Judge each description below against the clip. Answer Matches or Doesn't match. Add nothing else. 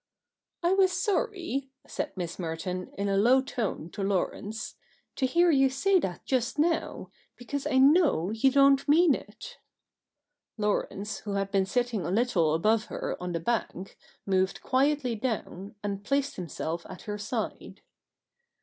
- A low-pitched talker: Doesn't match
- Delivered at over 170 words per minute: Doesn't match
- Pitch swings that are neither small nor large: Doesn't match